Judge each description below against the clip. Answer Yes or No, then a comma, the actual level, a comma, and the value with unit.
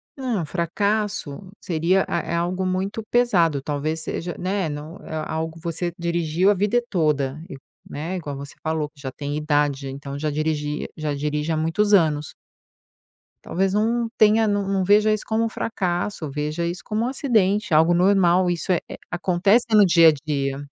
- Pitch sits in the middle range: Yes, medium, 170 Hz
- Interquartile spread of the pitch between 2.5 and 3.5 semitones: No, average, 4.9 semitones